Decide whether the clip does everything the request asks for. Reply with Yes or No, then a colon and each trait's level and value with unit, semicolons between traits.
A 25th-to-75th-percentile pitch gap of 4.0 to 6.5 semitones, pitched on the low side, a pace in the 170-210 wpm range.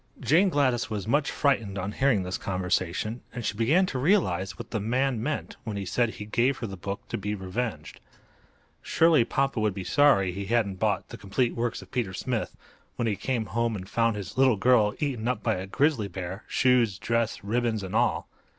Yes: average, 4.3 semitones; low, 115 Hz; average, 200 wpm